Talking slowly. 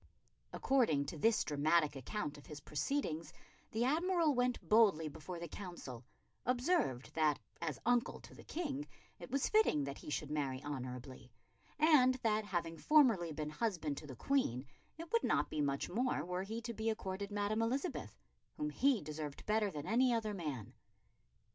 No: average, 165 wpm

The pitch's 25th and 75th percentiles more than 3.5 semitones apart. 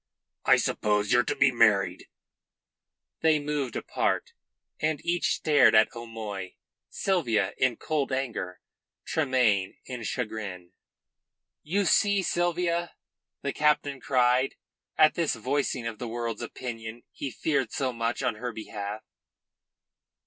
Yes: average, 4.9 semitones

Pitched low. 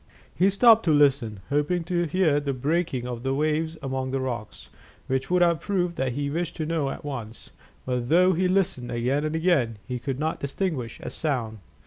No: medium, 145 Hz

